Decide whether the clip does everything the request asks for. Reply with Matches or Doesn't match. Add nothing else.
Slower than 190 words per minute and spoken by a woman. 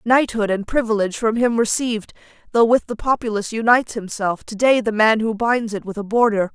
Doesn't match